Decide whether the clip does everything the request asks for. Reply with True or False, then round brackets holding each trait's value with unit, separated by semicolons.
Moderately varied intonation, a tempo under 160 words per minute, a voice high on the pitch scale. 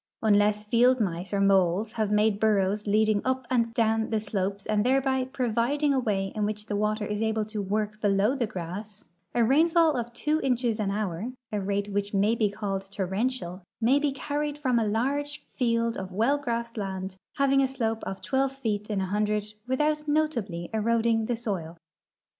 False (3.8 semitones; 185 wpm; 220 Hz)